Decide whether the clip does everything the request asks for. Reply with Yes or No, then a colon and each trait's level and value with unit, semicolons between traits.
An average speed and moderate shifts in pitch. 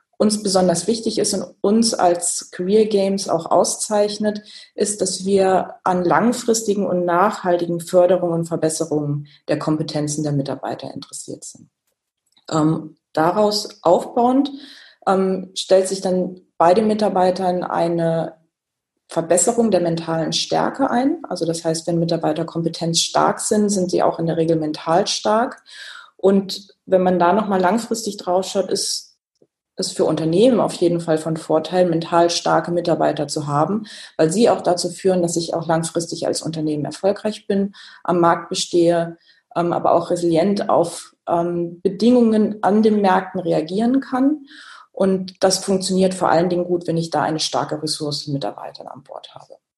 Yes: average, 150 wpm; average, 3.2 semitones